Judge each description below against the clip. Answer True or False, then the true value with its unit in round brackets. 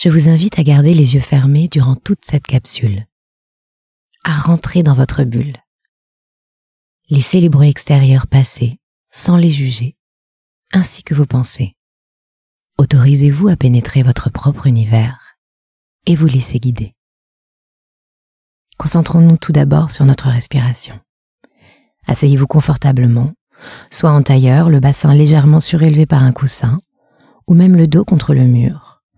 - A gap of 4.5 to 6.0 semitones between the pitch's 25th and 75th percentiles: False (3.7 semitones)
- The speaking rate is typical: False (130 wpm)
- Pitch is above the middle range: False (140 Hz)